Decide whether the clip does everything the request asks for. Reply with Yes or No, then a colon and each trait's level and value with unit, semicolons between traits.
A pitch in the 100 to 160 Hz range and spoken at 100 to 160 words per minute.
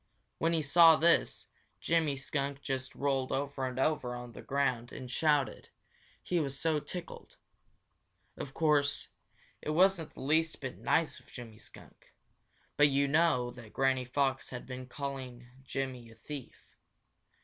Yes: medium, 140 Hz; average, 150 wpm